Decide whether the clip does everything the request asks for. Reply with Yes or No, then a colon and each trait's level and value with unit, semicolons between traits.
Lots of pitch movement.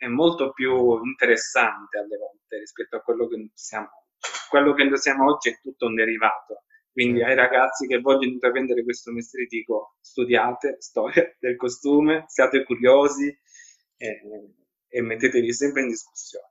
Yes: wide, 5.7 semitones